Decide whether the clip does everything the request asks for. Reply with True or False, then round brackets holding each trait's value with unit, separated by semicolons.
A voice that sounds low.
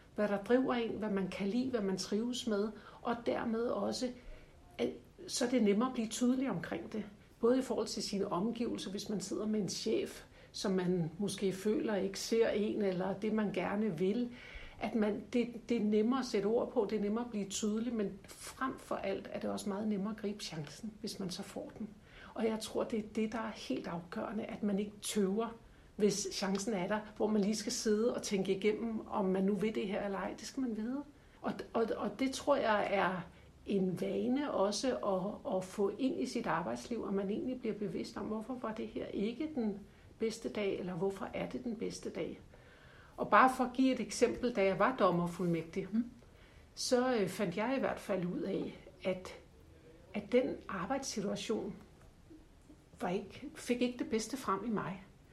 False (215 Hz)